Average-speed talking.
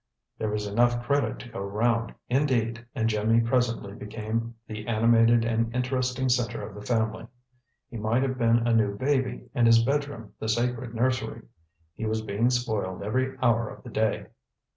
Yes: average, 170 wpm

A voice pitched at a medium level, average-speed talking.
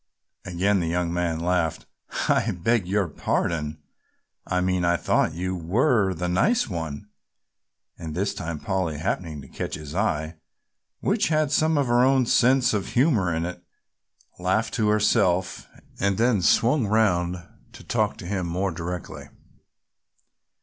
No: very low, 90 Hz; average, 150 wpm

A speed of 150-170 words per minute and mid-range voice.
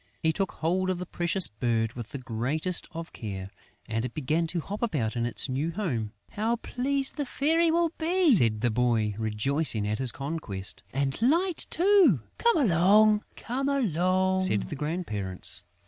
Yes: average, 165 wpm; medium, 160 Hz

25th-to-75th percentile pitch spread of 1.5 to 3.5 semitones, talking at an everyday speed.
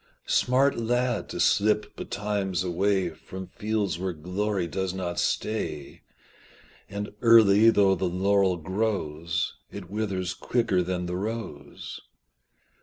No: average, 3.1 semitones; slow, 115 wpm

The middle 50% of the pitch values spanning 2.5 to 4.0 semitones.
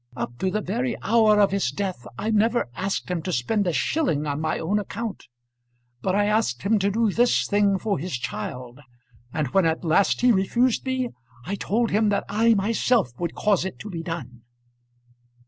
No: average, 5.1 semitones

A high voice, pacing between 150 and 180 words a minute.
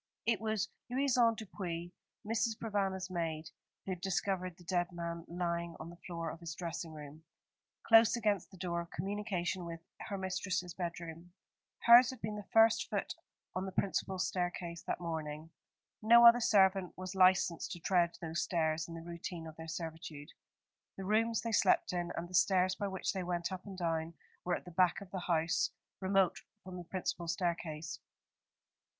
No: medium, 180 Hz; average, 175 wpm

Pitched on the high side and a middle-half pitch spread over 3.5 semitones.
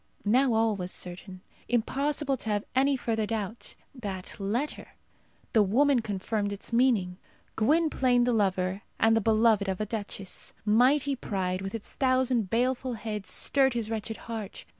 Yes: high, 225 Hz; average, 3.9 semitones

